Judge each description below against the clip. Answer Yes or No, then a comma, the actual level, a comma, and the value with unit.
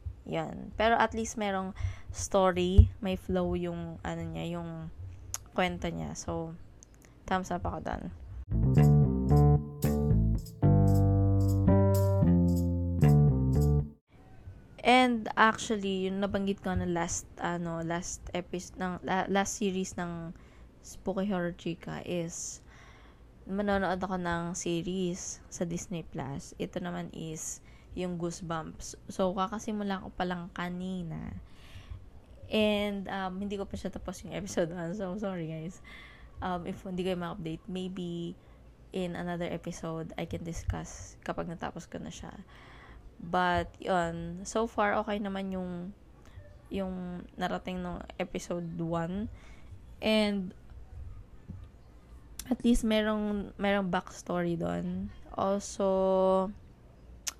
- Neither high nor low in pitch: Yes, medium, 175 Hz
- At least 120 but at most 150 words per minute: No, slow, 110 wpm